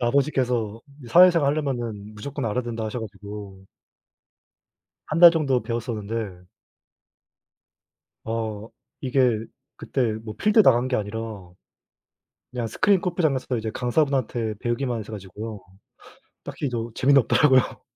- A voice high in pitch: No, low, 120 Hz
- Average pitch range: Yes, average, 3.9 semitones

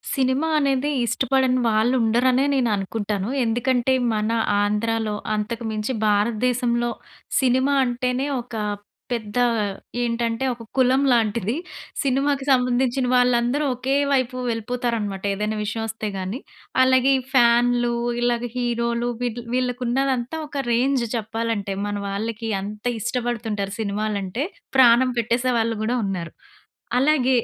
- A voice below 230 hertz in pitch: No, high, 240 Hz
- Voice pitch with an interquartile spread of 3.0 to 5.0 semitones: No, narrow, 2.6 semitones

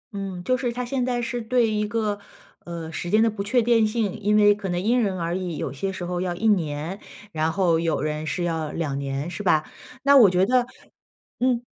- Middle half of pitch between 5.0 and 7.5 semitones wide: Yes, average, 5.3 semitones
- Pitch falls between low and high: No, high, 195 Hz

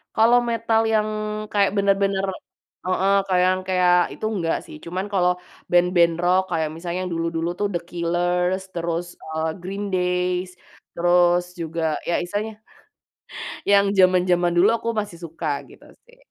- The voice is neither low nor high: Yes, medium, 180 Hz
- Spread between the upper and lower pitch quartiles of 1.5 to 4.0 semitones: Yes, narrow, 2.4 semitones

